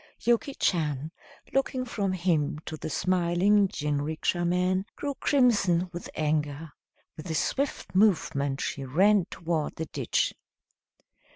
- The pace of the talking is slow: Yes, slow, 120 wpm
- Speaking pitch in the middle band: Yes, medium, 175 Hz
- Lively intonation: No, average, 4.5 semitones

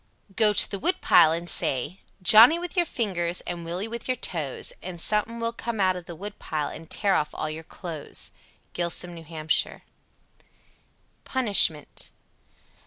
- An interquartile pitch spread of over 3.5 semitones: Yes, average, 5.2 semitones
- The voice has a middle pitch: Yes, medium, 180 Hz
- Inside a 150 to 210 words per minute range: Yes, average, 165 wpm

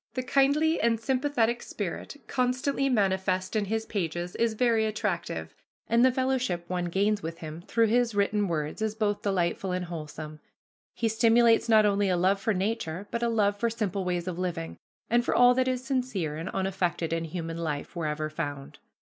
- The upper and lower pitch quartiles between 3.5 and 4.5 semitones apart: No, average, 5.2 semitones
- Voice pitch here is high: Yes, high, 205 Hz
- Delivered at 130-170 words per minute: No, average, 180 wpm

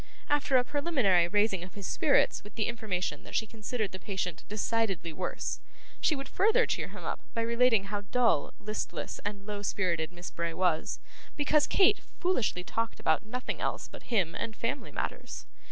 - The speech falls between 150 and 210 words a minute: Yes, average, 175 wpm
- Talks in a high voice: Yes, high, 215 Hz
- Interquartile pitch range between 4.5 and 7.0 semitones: Yes, average, 5.1 semitones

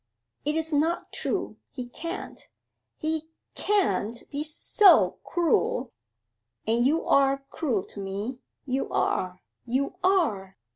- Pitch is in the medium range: No, very high, 275 Hz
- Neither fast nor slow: No, slow, 130 wpm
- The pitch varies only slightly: No, wide, 5.5 semitones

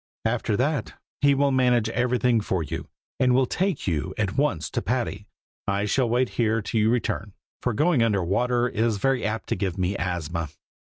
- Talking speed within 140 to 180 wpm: No, average, 200 wpm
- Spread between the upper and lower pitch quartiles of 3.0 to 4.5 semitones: Yes, average, 4.2 semitones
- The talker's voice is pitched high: No, low, 115 Hz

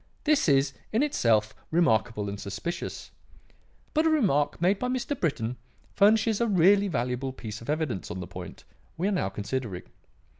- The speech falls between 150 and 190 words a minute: Yes, average, 160 wpm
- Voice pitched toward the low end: No, medium, 145 Hz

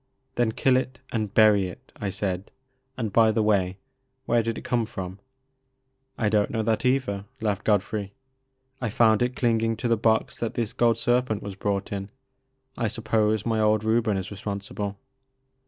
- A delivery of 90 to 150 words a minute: No, average, 185 wpm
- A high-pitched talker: No, low, 110 Hz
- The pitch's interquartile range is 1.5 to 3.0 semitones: Yes, narrow, 2.6 semitones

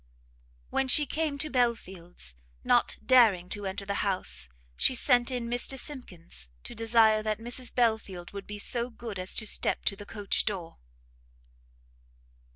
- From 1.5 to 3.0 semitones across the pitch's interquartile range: No, average, 4.0 semitones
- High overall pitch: Yes, high, 220 Hz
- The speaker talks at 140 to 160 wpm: Yes, average, 155 wpm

